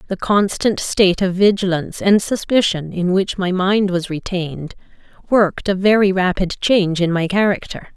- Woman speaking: Yes, female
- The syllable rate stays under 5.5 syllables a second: Yes, 5.0 syllables/s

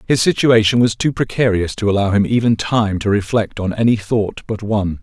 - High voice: No, low, 110 Hz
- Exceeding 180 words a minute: Yes, fast, 205 wpm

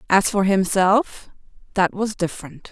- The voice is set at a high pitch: Yes, high, 195 Hz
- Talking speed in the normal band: No, slow, 110 wpm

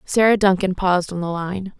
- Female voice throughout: Yes, female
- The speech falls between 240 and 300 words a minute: No, average, 200 wpm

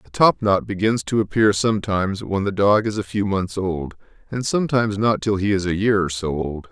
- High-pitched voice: No, low, 100 Hz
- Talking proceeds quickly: Yes, fast, 225 wpm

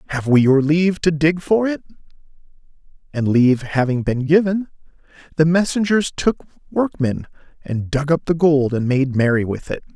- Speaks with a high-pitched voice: No, medium, 150 Hz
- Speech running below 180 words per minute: Yes, average, 165 wpm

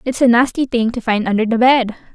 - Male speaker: No, female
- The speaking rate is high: Yes, fast, 250 wpm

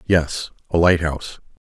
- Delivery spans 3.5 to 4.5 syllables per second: Yes, 4.3 syllables/s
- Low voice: Yes, very low, 80 Hz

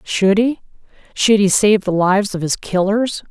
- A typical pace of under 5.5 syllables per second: Yes, 4.6 syllables/s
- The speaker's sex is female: Yes, female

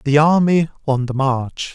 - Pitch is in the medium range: Yes, medium, 145 Hz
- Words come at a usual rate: Yes, average, 170 wpm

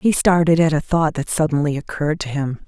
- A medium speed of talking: No, fast, 225 wpm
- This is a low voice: No, medium, 155 Hz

